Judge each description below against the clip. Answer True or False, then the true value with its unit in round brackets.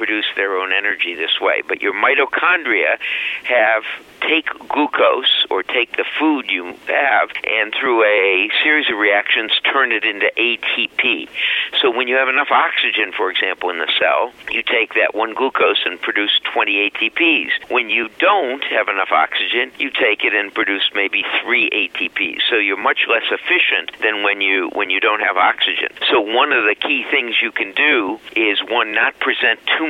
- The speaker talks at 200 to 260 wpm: False (180 wpm)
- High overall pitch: True (325 Hz)